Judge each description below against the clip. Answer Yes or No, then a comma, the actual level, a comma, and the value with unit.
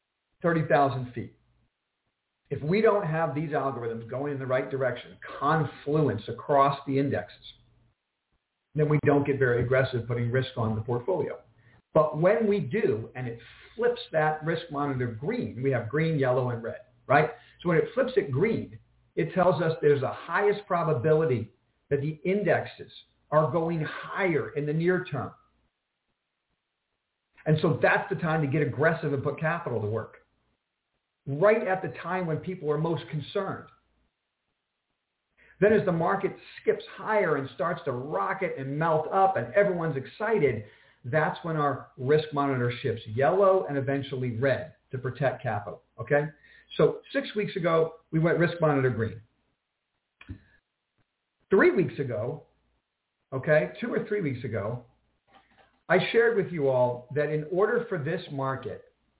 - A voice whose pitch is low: No, medium, 150 Hz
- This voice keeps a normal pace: Yes, average, 150 wpm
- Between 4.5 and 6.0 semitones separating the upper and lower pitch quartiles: Yes, average, 5.1 semitones